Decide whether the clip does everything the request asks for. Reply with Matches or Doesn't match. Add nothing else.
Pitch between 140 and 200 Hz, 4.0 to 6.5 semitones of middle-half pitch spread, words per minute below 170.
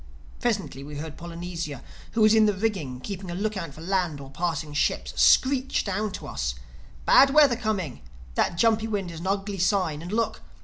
Doesn't match